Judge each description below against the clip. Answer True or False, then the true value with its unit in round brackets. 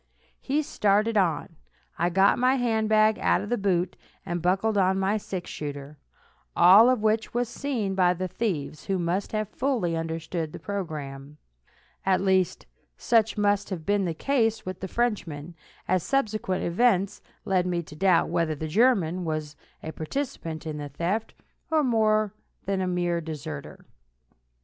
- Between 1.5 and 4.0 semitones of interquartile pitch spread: False (4.5 semitones)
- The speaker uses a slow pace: False (160 wpm)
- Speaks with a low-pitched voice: False (190 Hz)